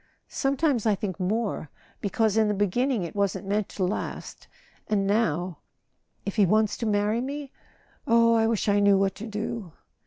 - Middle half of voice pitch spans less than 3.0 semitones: Yes, narrow, 2.6 semitones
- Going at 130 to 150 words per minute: No, average, 160 wpm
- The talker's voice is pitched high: Yes, high, 210 Hz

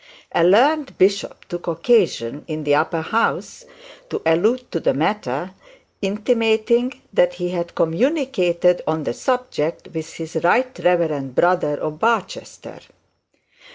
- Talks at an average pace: No, slow, 125 wpm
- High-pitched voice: No, medium, 180 Hz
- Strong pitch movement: Yes, wide, 6.0 semitones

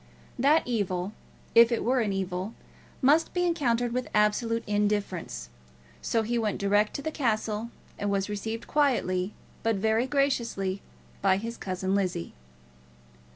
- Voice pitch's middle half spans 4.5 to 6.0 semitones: No, average, 3.5 semitones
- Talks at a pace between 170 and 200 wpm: No, average, 140 wpm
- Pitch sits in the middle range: No, high, 215 Hz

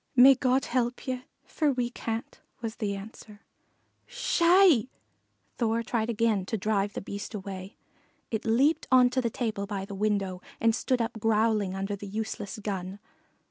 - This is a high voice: Yes, high, 220 Hz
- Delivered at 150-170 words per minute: Yes, average, 165 wpm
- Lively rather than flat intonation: No, average, 3.4 semitones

